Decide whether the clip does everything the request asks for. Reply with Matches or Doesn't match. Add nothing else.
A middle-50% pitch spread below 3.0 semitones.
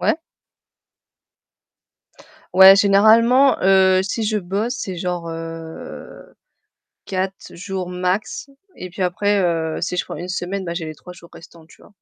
Matches